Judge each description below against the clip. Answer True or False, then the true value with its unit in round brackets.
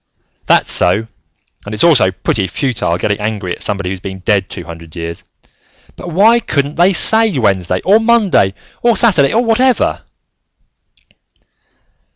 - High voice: False (110 Hz)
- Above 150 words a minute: False (145 wpm)